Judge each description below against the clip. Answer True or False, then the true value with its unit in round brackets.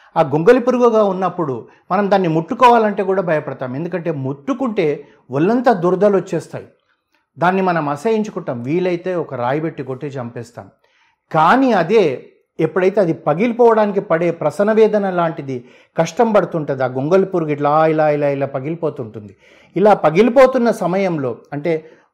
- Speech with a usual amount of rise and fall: False (5.9 semitones)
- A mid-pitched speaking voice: True (170 Hz)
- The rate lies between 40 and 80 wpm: False (120 wpm)